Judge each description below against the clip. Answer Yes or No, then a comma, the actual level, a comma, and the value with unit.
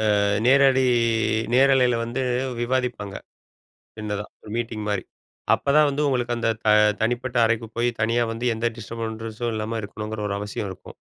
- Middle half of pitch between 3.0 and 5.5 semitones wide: No, narrow, 2.6 semitones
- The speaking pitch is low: Yes, low, 115 Hz